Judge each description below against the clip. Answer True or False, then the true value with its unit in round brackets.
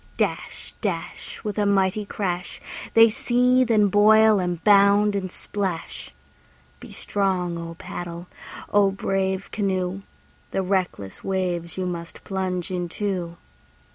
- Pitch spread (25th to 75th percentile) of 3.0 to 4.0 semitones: False (2.4 semitones)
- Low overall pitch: False (190 Hz)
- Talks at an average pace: False (120 wpm)